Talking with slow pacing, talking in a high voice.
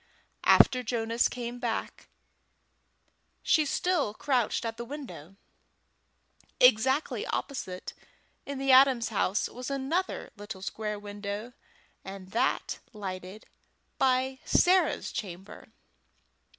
Yes: slow, 95 wpm; high, 230 Hz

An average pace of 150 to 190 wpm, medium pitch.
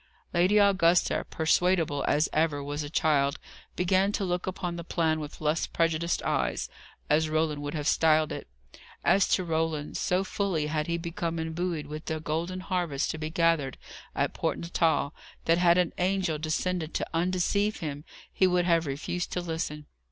Yes: average, 170 wpm; medium, 165 Hz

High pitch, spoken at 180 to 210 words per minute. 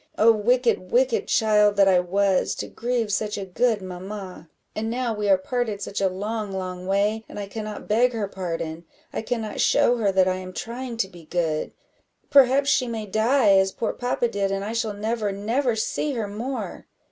Yes: high, 210 Hz; average, 195 wpm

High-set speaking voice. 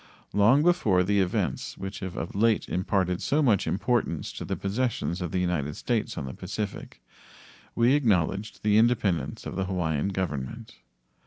No: very low, 95 Hz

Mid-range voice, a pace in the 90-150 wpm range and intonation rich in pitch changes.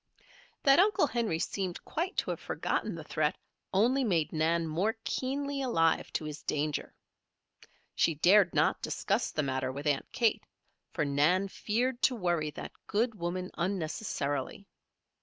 Yes: medium, 180 Hz; average, 145 wpm; wide, 7.3 semitones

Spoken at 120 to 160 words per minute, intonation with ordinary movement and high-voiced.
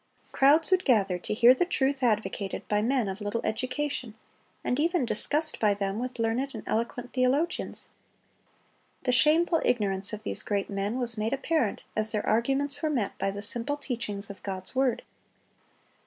No: average, 170 wpm; average, 4.8 semitones; high, 240 Hz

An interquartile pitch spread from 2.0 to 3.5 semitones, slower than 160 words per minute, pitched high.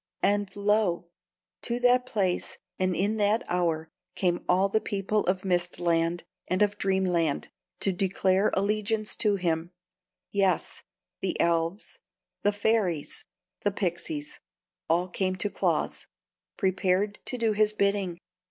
Yes: average, 2.8 semitones; slow, 135 wpm; high, 195 Hz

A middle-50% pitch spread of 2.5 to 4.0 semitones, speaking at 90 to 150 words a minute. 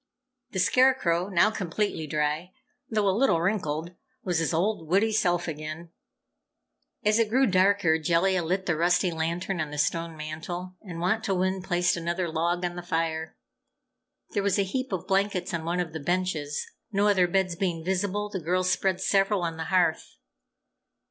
No: average, 2.9 semitones; average, 170 wpm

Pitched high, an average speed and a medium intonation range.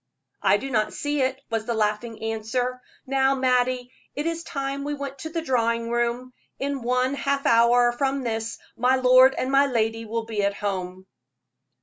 Yes: very high, 250 Hz; average, 180 wpm; average, 3.1 semitones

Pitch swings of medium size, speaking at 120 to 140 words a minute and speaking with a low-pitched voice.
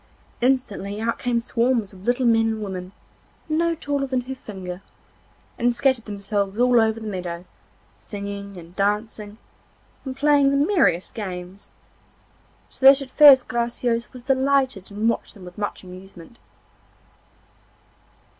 No: average, 4.7 semitones; slow, 135 wpm; high, 225 Hz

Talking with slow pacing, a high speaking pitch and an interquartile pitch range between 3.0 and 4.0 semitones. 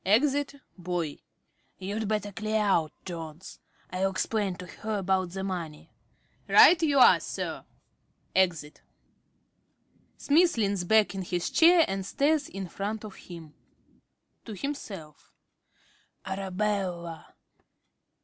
Yes: slow, 120 wpm; high, 195 Hz; average, 3.6 semitones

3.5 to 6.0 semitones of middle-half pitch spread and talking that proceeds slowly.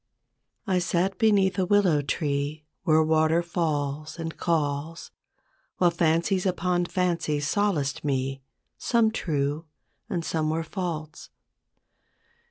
No: average, 3.1 semitones; slow, 110 wpm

